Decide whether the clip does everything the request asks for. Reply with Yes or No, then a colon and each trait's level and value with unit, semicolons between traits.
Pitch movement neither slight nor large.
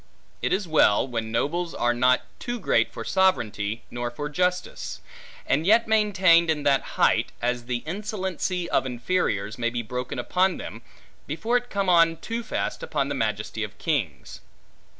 No: wide, 7.7 semitones